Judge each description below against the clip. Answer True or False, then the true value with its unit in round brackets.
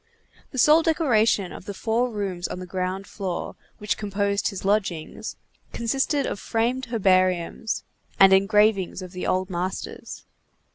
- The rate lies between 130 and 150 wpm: True (140 wpm)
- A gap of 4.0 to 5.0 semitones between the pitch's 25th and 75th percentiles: False (3.4 semitones)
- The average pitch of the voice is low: False (200 Hz)